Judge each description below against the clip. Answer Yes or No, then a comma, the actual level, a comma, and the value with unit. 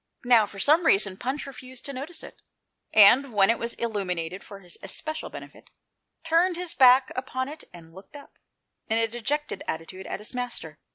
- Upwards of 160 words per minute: Yes, average, 180 wpm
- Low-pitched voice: No, high, 240 Hz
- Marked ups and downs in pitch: Yes, wide, 6.1 semitones